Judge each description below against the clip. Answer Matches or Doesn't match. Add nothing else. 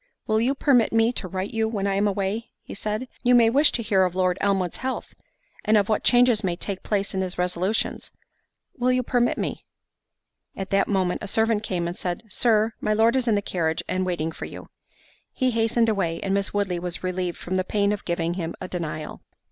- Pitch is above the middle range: Matches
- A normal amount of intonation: Matches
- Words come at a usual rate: Doesn't match